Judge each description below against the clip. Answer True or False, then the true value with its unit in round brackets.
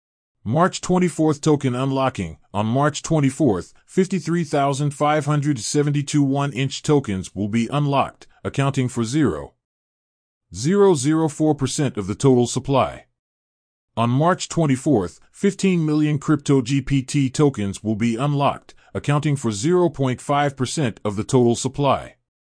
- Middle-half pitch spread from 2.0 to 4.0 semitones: False (4.5 semitones)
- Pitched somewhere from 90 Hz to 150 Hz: True (140 Hz)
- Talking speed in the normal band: False (110 wpm)